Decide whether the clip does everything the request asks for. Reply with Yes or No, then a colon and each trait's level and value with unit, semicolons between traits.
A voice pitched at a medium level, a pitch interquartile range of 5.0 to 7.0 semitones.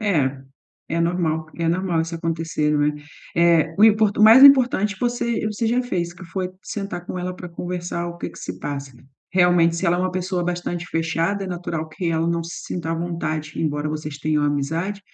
No: medium, 170 Hz; narrow, 2.4 semitones